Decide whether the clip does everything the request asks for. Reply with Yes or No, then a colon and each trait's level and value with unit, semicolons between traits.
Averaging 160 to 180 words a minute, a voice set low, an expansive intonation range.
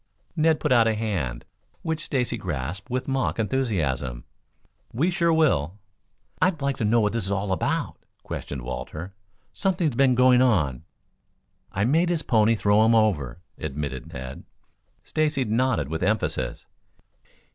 No: average, 145 wpm; low, 110 Hz; wide, 8.8 semitones